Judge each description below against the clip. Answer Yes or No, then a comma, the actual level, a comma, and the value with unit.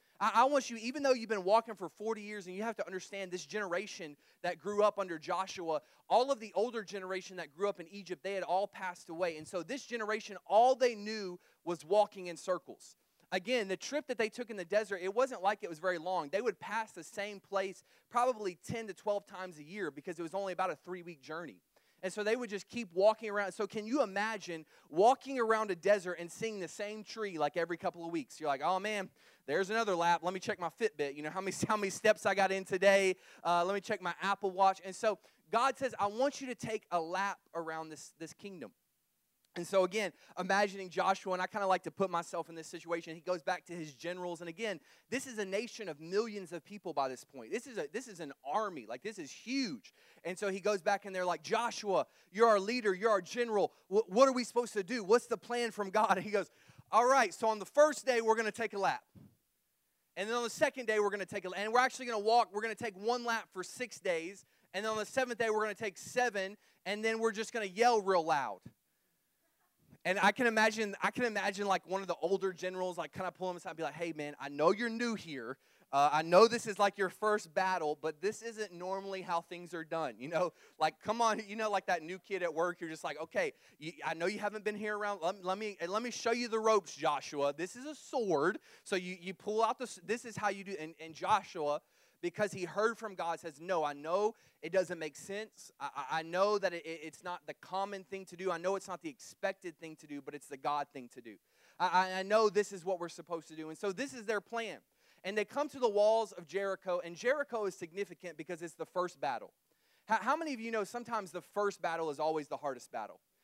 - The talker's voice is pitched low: No, high, 195 Hz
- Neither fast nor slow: No, fast, 250 wpm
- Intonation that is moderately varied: Yes, average, 3.9 semitones